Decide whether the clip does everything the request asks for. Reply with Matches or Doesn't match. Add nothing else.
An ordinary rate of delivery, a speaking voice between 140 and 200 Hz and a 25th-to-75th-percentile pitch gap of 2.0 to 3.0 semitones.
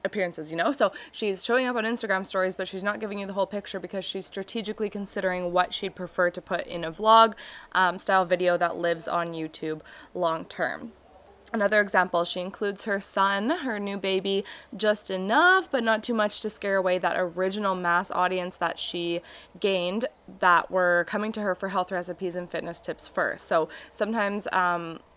Matches